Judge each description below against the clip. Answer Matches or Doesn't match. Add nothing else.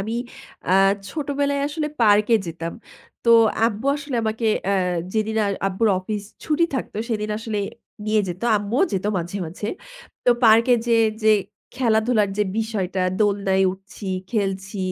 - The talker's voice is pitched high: Matches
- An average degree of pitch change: Matches